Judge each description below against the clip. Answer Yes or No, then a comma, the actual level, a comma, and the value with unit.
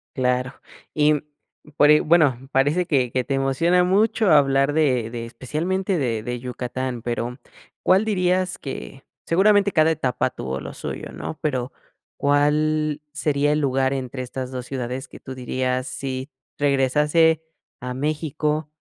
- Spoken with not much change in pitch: No, average, 3.3 semitones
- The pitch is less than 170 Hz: Yes, medium, 140 Hz